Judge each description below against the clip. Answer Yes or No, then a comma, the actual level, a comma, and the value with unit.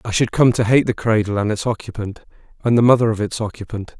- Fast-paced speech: Yes, fast, 240 wpm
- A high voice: No, low, 110 Hz